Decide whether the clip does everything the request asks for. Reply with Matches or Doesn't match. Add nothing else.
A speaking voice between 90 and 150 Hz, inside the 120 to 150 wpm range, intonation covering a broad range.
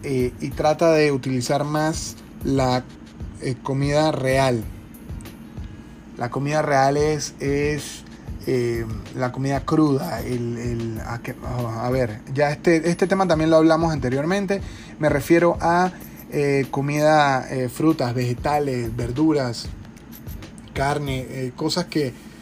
Doesn't match